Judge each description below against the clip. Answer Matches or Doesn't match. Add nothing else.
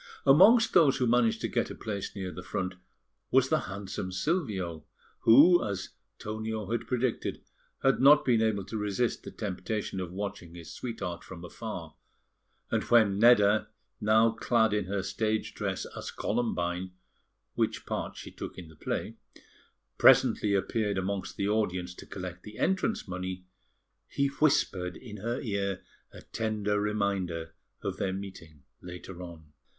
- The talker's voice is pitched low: Matches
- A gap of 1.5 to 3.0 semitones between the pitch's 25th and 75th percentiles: Doesn't match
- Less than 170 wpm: Matches